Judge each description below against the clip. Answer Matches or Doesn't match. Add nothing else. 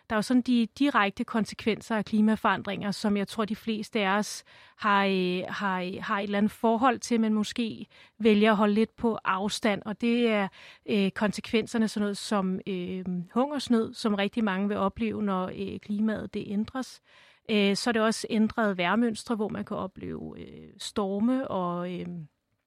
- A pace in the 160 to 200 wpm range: Matches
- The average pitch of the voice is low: Doesn't match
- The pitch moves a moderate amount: Doesn't match